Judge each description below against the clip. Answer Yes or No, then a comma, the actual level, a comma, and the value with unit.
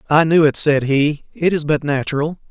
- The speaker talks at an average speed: No, fast, 215 wpm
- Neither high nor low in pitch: Yes, medium, 150 Hz